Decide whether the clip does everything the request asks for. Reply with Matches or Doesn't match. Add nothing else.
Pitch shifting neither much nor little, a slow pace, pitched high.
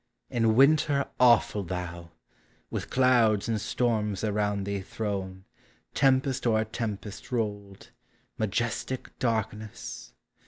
Doesn't match